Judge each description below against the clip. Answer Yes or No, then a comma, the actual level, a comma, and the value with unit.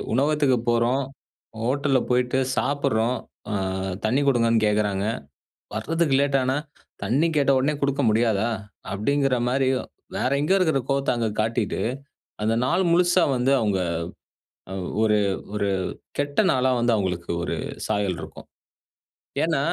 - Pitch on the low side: Yes, low, 130 Hz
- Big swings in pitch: No, average, 4.2 semitones